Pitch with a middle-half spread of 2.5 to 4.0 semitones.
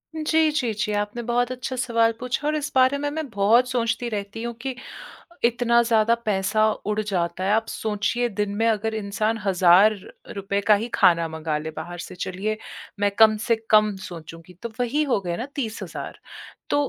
Yes: average, 3.3 semitones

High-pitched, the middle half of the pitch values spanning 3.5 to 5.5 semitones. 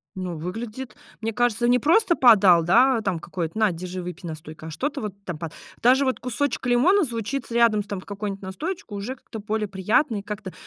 Yes: high, 215 Hz; average, 4.9 semitones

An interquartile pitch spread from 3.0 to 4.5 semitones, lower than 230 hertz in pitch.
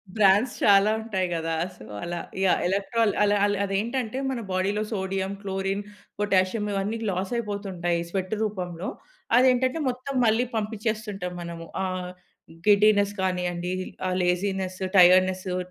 No: narrow, 2.6 semitones; high, 195 Hz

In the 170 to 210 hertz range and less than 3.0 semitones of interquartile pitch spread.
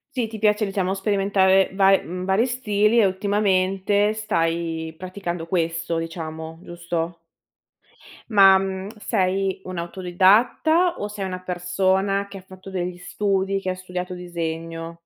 Yes: high, 190 Hz; narrow, 2.4 semitones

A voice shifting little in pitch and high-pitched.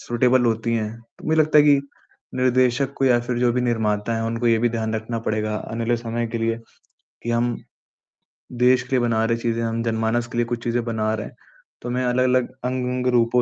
No: narrow, 1.6 semitones; low, 120 Hz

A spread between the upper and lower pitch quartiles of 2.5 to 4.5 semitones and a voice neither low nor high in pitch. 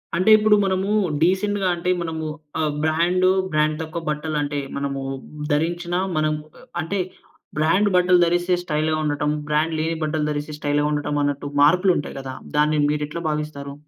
Yes: average, 2.9 semitones; medium, 155 Hz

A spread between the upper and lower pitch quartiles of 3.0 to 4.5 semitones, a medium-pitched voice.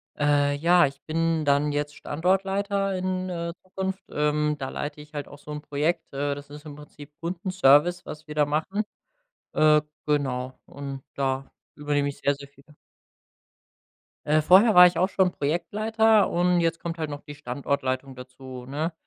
Yes: average, 3.7 semitones; medium, 150 Hz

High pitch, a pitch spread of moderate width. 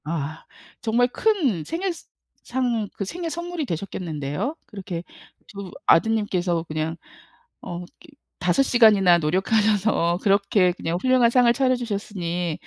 No: high, 200 Hz; wide, 6.1 semitones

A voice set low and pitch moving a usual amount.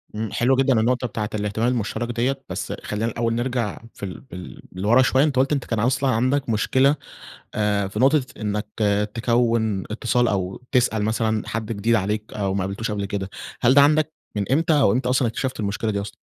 Yes: low, 115 Hz; average, 3.6 semitones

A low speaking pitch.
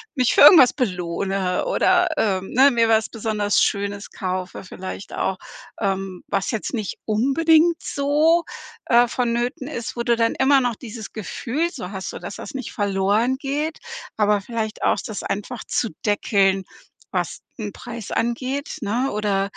No: high, 225 Hz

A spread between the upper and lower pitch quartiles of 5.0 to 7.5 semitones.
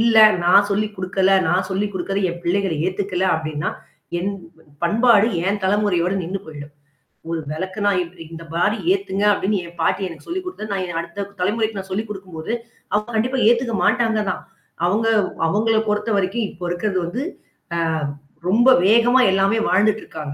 No: average, 3.4 semitones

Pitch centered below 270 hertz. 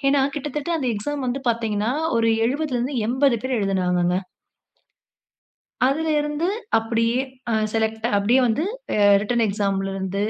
Yes: high, 235 Hz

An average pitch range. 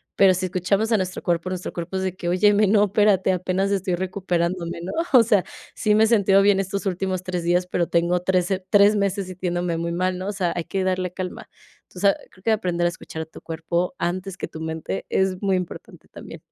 No: narrow, 2.1 semitones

